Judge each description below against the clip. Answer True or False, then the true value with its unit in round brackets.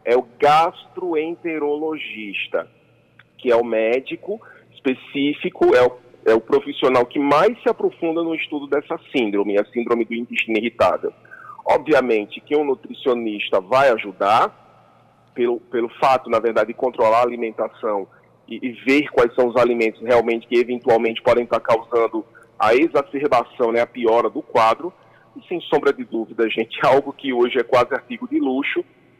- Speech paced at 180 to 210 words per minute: False (155 wpm)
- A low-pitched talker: True (125 Hz)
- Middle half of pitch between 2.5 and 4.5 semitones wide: False (5.0 semitones)